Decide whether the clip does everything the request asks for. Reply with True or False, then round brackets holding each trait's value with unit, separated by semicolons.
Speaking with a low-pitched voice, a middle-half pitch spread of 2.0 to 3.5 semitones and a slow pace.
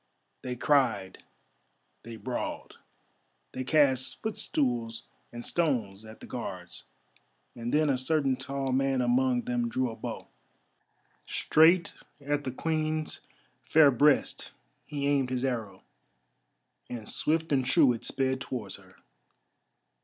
True (130 Hz; 3.2 semitones; 125 wpm)